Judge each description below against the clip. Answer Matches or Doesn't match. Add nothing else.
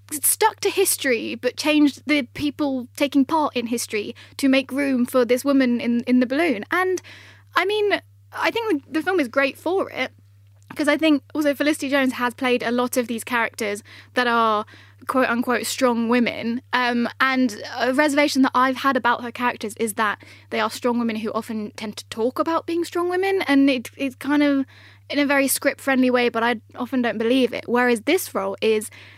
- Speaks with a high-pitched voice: Matches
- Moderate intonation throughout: Matches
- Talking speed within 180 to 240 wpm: Matches